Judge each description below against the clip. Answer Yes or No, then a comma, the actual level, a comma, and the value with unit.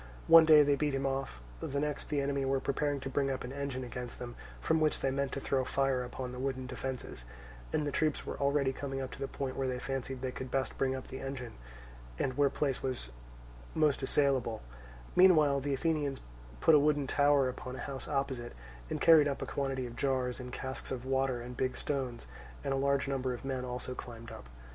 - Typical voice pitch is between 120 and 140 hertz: Yes, low, 135 Hz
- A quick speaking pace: Yes, fast, 220 wpm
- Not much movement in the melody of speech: Yes, narrow, 1.7 semitones